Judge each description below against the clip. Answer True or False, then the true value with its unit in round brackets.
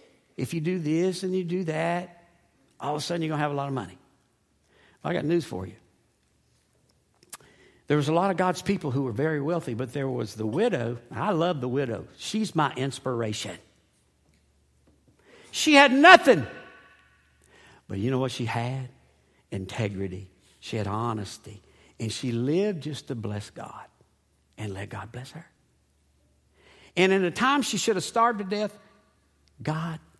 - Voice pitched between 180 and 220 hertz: False (130 Hz)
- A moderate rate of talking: True (170 wpm)